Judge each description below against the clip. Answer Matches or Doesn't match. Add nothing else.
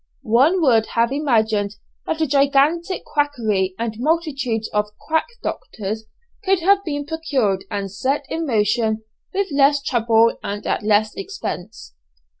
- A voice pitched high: Matches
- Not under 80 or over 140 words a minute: Matches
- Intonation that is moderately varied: Doesn't match